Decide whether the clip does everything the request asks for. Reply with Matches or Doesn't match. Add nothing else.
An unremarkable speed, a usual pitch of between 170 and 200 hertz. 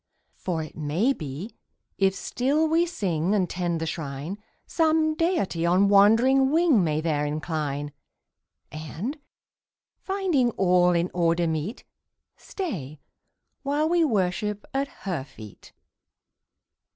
Doesn't match